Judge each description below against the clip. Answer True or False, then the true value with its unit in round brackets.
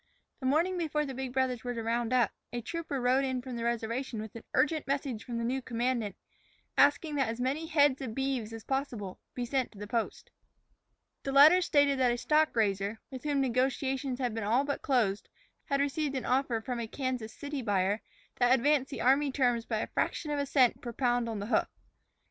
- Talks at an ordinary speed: False (215 wpm)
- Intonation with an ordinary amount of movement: True (3.1 semitones)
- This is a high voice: True (255 Hz)